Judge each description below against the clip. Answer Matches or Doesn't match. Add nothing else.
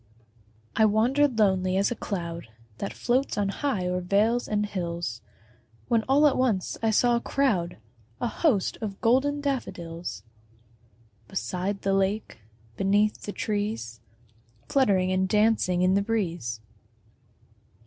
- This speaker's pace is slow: Matches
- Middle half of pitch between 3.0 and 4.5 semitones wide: Matches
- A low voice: Doesn't match